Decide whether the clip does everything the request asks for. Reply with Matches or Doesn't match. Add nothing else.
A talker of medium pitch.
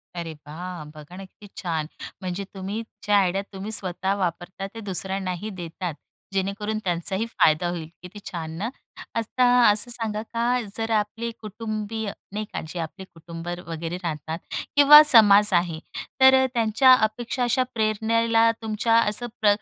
Doesn't match